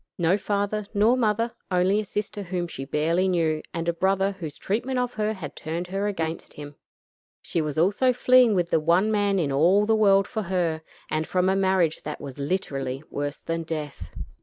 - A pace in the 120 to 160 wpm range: No, average, 200 wpm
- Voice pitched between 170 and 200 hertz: Yes, medium, 185 Hz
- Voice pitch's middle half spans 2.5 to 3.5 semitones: No, average, 4.3 semitones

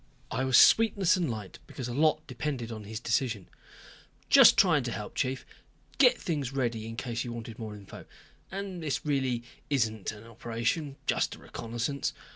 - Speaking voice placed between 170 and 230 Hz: No, low, 125 Hz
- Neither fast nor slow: Yes, average, 170 wpm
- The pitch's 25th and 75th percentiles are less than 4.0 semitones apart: No, average, 4.3 semitones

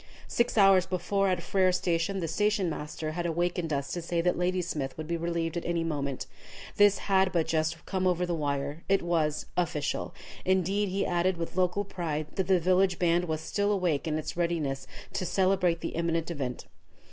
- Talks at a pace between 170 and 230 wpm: Yes, average, 190 wpm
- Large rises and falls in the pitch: No, narrow, 2.6 semitones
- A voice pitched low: No, medium, 175 Hz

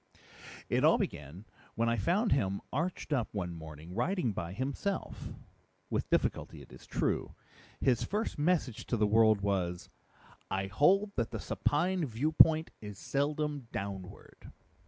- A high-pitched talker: No, low, 115 Hz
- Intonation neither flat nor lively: No, wide, 7.7 semitones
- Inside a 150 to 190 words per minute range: No, average, 140 wpm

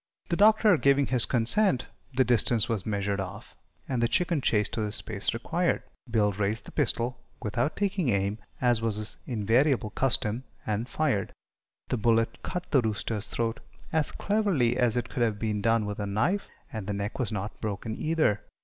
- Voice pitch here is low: Yes, low, 115 Hz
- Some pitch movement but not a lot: Yes, average, 4.2 semitones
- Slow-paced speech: No, average, 180 wpm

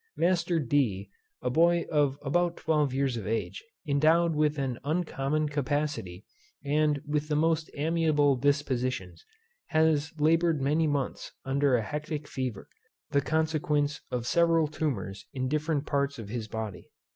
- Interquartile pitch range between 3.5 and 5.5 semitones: No, average, 3.0 semitones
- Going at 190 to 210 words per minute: No, average, 140 wpm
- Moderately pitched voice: Yes, medium, 145 Hz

